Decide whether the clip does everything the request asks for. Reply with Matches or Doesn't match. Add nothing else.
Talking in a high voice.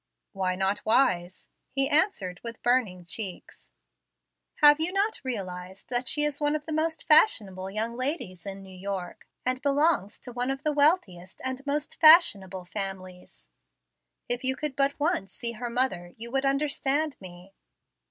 Matches